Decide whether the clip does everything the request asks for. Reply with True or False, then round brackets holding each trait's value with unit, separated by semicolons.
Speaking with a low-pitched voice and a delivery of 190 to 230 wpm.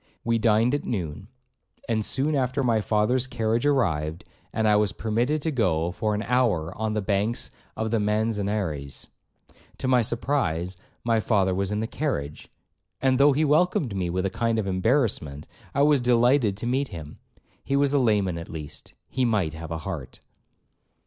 False (110 Hz; 175 wpm)